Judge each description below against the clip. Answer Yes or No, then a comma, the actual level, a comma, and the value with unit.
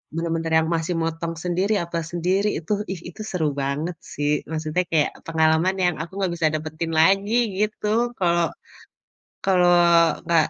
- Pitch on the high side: No, medium, 170 Hz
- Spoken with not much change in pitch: Yes, narrow, 2.2 semitones